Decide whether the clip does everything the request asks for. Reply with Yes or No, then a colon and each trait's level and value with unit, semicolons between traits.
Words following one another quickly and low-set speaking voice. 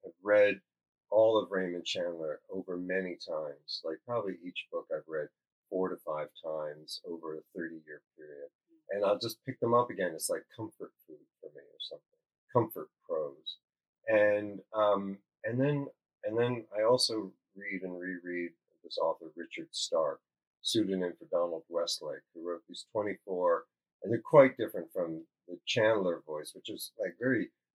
No: average, 160 wpm; low, 120 Hz